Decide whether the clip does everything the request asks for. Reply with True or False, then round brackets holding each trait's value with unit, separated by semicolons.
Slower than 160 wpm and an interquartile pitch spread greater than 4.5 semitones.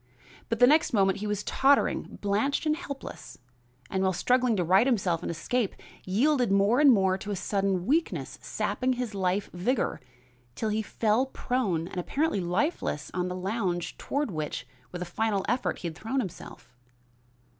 False (170 wpm; 5.3 semitones)